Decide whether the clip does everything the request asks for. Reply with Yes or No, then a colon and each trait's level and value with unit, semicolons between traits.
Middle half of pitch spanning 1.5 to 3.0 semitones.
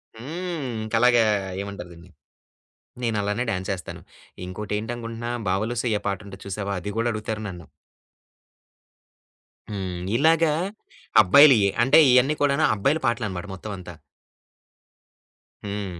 No: average, 3.8 semitones